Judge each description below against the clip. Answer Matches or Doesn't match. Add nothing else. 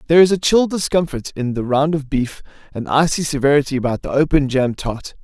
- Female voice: Doesn't match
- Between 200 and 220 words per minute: Matches